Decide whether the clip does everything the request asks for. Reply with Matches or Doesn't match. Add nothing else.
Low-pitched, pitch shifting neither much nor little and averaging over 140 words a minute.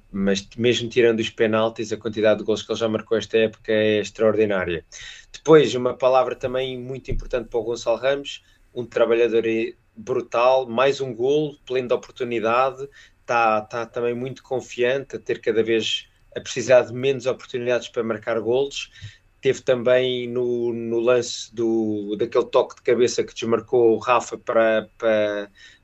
Doesn't match